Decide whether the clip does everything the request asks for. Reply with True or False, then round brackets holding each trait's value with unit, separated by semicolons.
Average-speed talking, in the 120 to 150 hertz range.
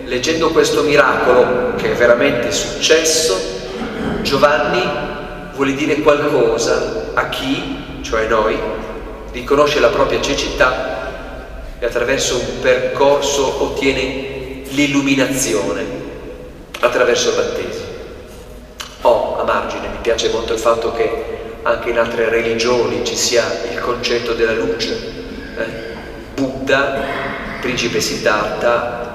False (105 wpm; 140 Hz)